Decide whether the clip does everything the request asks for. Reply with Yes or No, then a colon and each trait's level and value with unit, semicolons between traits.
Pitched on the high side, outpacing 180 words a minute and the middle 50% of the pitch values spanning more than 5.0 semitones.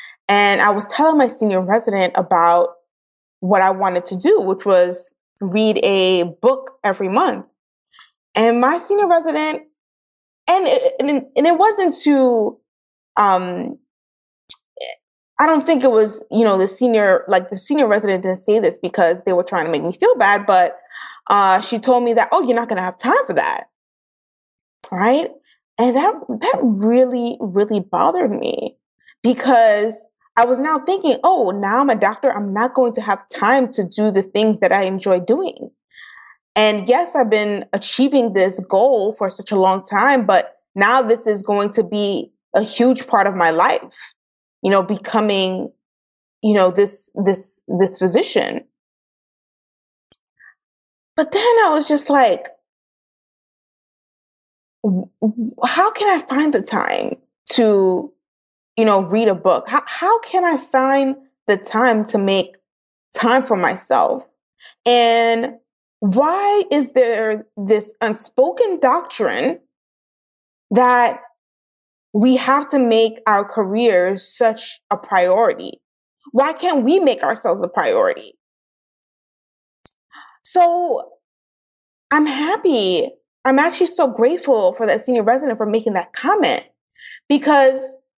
No: high, 230 Hz; average, 140 wpm; wide, 5.4 semitones